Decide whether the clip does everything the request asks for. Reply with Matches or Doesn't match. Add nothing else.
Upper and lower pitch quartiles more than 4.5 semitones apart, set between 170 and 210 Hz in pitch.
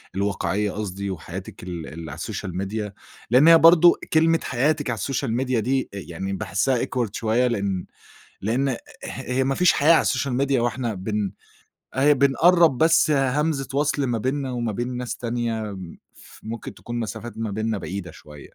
Doesn't match